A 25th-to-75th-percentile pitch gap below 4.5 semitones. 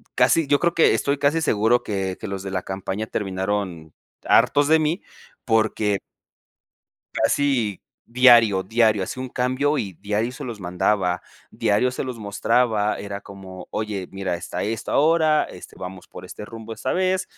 No: average, 5.0 semitones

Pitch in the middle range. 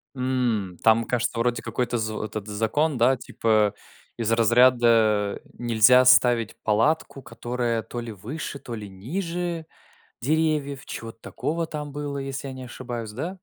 No: low, 120 Hz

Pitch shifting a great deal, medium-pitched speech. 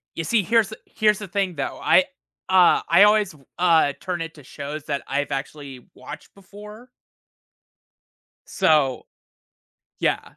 Yes: wide, 5.9 semitones; medium, 175 Hz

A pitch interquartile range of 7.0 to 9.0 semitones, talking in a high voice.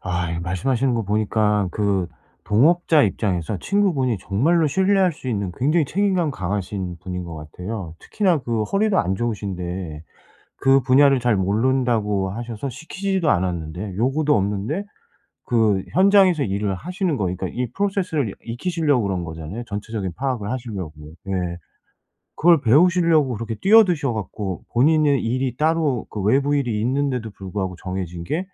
No: wide, 7.6 semitones; low, 115 Hz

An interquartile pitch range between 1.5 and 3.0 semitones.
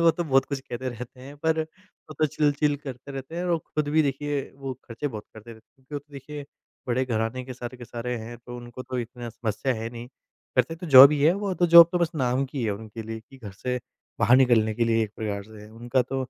No: average, 3.8 semitones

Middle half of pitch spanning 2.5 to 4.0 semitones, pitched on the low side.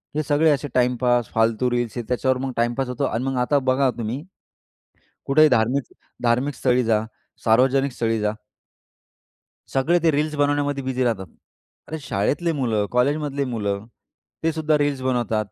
Yes: average, 3.5 semitones; low, 130 Hz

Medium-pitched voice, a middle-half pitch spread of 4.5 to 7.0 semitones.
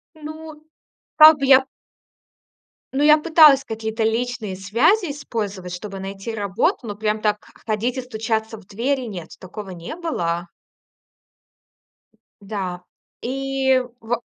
No: high, 225 Hz; average, 5.2 semitones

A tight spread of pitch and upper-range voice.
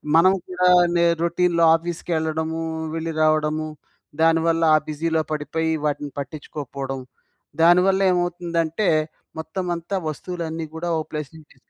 No: narrow, 1.9 semitones; medium, 165 Hz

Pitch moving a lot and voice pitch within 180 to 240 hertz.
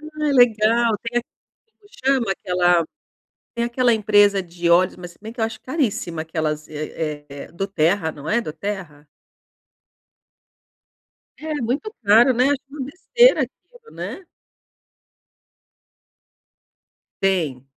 Yes: wide, 6.7 semitones; high, 210 Hz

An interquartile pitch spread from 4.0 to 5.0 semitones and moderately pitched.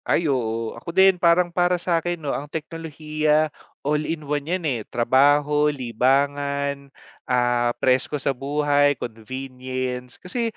No: average, 3.5 semitones; medium, 145 Hz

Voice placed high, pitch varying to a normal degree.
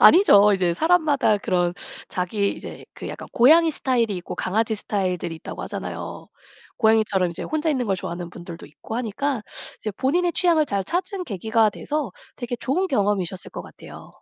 No: high, 220 Hz; wide, 7.5 semitones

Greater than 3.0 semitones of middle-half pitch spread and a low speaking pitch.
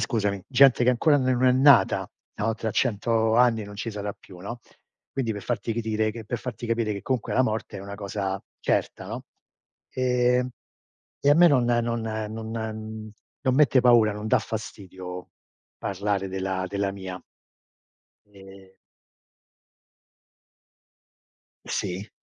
Yes: average, 3.5 semitones; low, 110 Hz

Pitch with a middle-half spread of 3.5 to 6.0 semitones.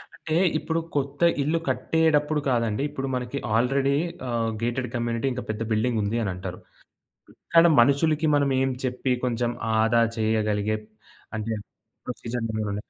Yes: average, 3.8 semitones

